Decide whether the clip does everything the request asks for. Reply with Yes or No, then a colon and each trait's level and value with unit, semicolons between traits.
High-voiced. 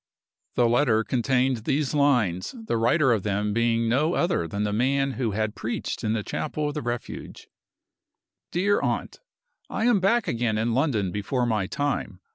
No: low, 120 Hz